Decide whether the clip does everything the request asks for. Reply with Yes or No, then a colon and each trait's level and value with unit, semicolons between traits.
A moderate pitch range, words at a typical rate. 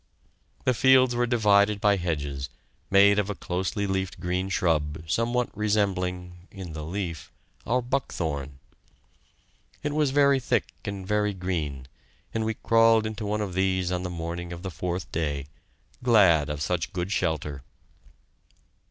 Yes: average, 4.1 semitones; average, 150 wpm